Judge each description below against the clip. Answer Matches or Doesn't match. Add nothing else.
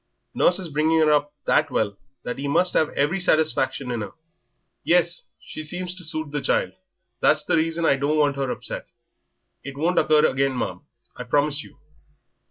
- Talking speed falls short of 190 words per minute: Matches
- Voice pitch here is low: Doesn't match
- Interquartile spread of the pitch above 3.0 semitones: Doesn't match